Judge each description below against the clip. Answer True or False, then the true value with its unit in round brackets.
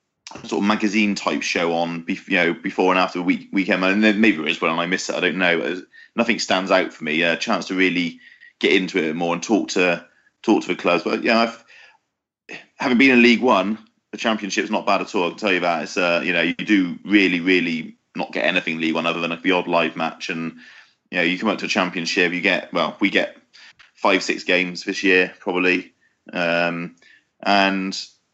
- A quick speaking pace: True (230 wpm)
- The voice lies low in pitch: True (90 Hz)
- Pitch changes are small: False (4.0 semitones)